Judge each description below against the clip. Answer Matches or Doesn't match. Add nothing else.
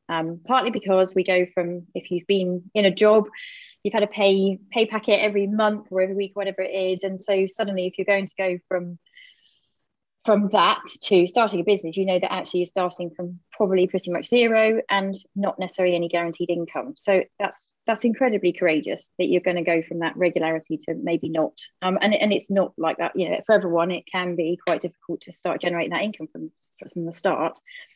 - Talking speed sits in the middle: Doesn't match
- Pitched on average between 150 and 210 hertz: Matches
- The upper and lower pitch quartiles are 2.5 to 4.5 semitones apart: Matches